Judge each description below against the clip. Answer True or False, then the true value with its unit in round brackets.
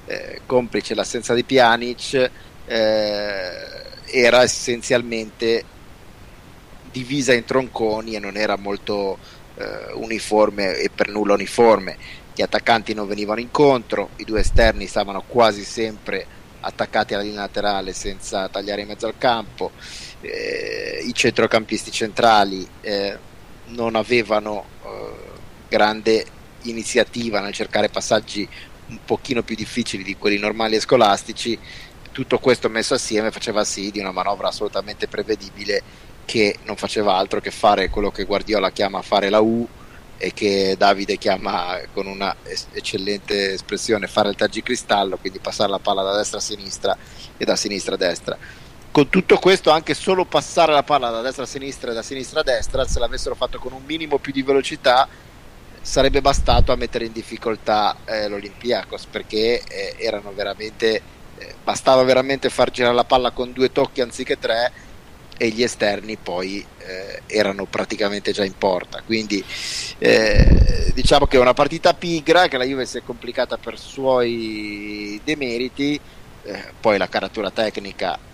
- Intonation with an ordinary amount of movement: True (4.1 semitones)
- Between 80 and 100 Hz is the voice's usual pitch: False (115 Hz)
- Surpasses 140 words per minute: True (150 wpm)